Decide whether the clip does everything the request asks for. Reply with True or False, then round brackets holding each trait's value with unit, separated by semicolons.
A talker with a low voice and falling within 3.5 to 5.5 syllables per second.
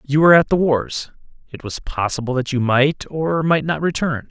False (145 Hz; 4.9 syllables/s)